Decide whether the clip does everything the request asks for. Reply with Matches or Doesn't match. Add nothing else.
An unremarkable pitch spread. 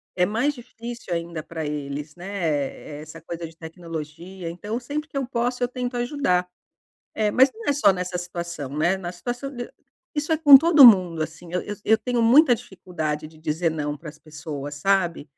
Doesn't match